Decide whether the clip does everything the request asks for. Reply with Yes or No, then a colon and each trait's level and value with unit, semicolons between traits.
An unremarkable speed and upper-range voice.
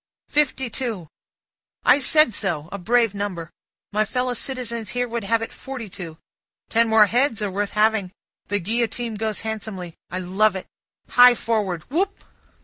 Yes: average, 155 wpm; high, 220 Hz